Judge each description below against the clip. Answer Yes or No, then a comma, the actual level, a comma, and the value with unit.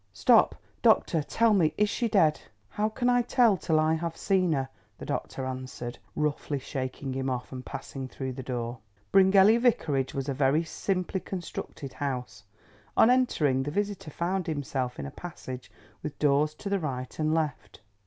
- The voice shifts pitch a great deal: Yes, wide, 6.4 semitones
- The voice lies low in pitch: No, medium, 150 Hz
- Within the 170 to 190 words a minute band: Yes, average, 175 wpm